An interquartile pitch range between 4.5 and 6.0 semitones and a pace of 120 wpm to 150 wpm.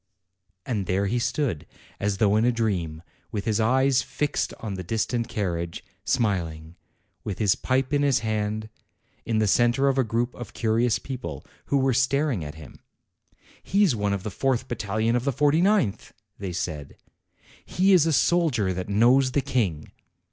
No: average, 5.1 semitones; average, 170 wpm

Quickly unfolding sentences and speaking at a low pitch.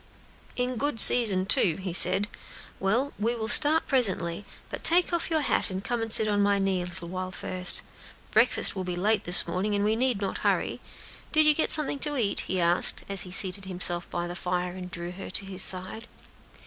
No: fast, 210 wpm; high, 195 Hz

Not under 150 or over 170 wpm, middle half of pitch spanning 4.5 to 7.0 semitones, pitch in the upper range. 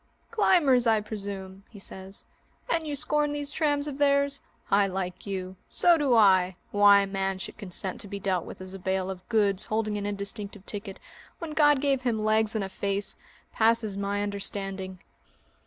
No: average, 180 wpm; average, 5.0 semitones; high, 205 Hz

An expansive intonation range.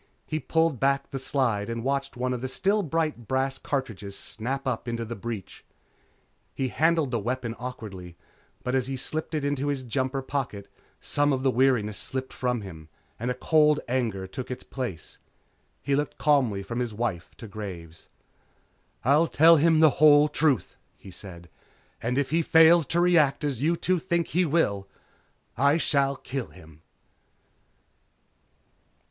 No: average, 4.4 semitones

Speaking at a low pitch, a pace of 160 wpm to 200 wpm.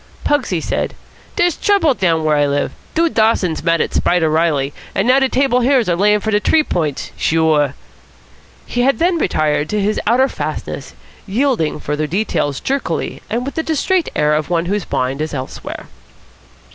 No: high, 195 Hz; average, 175 wpm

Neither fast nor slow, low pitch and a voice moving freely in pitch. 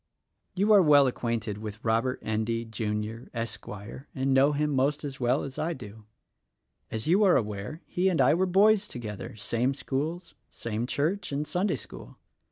Yes: average, 170 wpm; low, 130 Hz; wide, 5.7 semitones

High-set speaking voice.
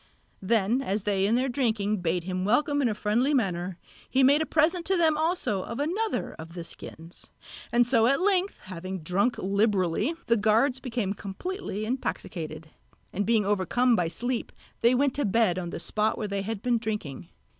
Yes: high, 220 Hz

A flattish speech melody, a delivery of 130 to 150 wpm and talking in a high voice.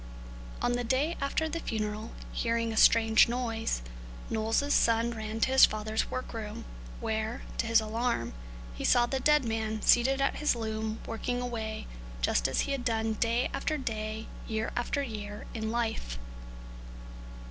No: narrow, 2.1 semitones; average, 160 wpm; high, 225 Hz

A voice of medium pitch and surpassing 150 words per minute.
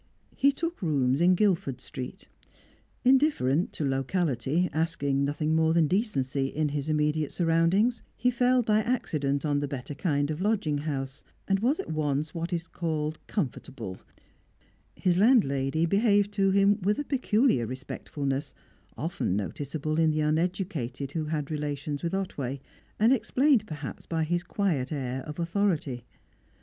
No: medium, 160 Hz; average, 145 wpm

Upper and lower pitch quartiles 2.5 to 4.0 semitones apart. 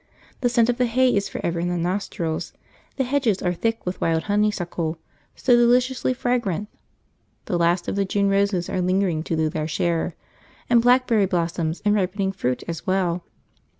No: average, 5.2 semitones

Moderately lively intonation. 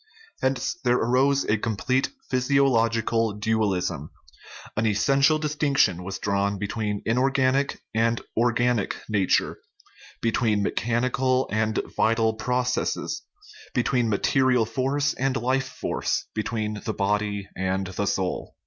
Yes: average, 3.7 semitones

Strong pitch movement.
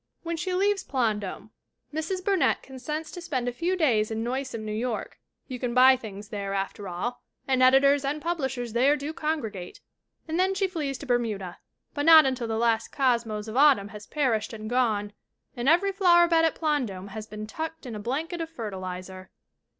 Yes: wide, 6.5 semitones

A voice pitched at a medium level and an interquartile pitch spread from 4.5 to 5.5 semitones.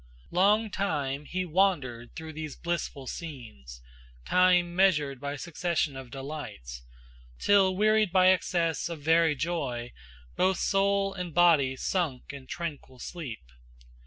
Yes: medium, 160 Hz; average, 5.2 semitones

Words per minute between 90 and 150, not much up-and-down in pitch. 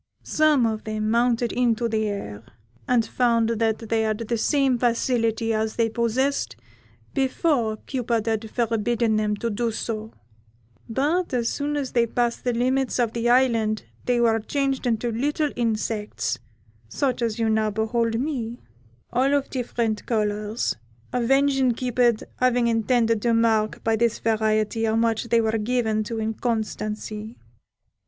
Yes: average, 145 wpm; narrow, 2.1 semitones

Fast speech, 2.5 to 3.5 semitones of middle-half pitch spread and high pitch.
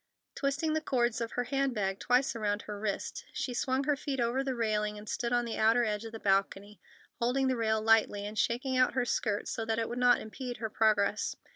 Yes: fast, 230 wpm; average, 3.1 semitones; high, 230 Hz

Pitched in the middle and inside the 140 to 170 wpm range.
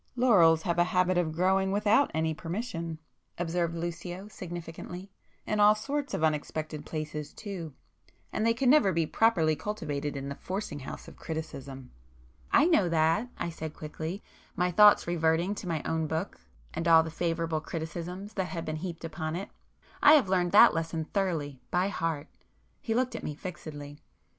Yes: medium, 170 Hz; average, 160 wpm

